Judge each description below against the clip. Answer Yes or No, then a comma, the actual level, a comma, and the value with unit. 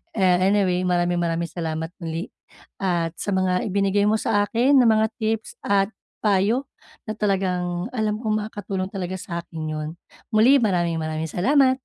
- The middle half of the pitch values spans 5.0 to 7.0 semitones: No, average, 3.6 semitones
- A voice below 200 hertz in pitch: Yes, high, 190 Hz